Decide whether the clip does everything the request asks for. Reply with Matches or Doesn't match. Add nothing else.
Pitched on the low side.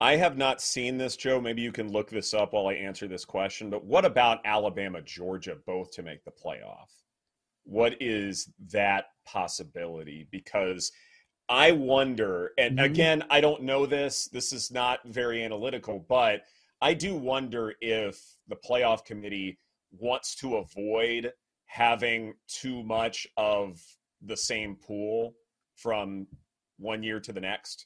Matches